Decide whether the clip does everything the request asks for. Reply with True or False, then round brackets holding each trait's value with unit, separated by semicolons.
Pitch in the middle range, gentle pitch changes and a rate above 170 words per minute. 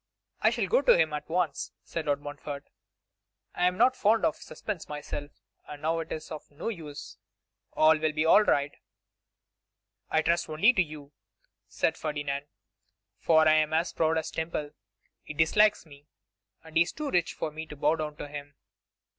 True (155 Hz; 2.3 semitones; 180 wpm)